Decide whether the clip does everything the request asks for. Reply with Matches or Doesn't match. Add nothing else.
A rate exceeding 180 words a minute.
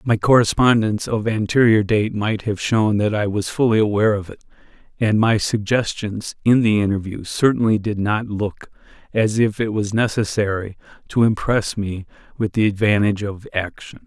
Doesn't match